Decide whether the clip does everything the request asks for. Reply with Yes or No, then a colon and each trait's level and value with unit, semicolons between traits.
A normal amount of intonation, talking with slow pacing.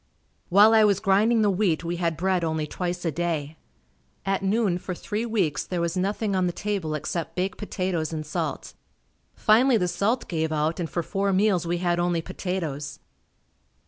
No: average, 3.2 semitones; average, 180 wpm